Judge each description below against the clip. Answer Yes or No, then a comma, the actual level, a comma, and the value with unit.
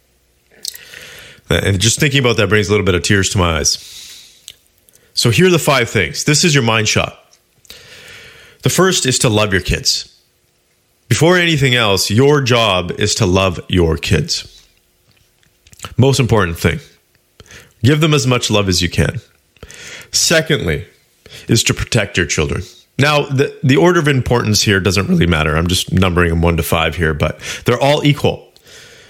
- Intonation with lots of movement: Yes, wide, 6.9 semitones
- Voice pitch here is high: No, low, 110 Hz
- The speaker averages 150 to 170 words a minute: Yes, average, 165 wpm